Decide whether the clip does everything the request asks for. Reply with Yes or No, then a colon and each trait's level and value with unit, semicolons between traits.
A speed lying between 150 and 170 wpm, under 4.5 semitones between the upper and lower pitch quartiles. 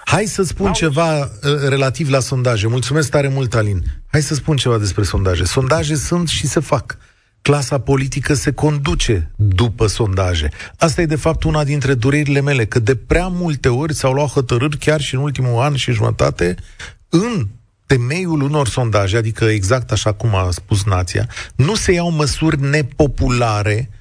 No: average, 165 wpm; wide, 5.5 semitones